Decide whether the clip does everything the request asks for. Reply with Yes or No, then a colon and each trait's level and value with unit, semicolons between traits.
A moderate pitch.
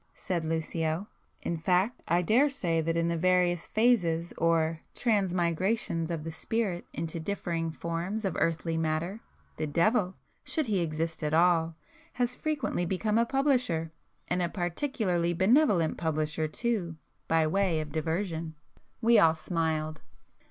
Yes: medium, 170 Hz